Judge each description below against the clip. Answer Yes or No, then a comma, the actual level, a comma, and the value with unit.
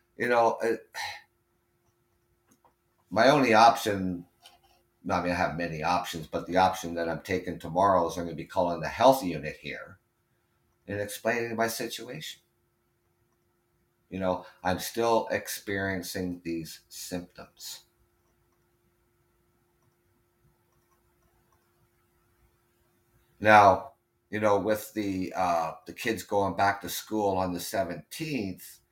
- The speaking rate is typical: No, slow, 110 wpm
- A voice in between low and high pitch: No, very low, 95 Hz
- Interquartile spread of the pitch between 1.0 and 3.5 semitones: No, average, 4.1 semitones